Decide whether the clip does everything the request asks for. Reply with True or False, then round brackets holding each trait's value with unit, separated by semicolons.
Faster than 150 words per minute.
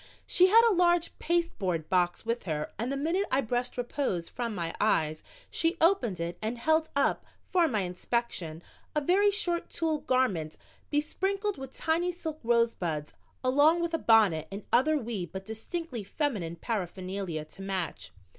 True (160 wpm)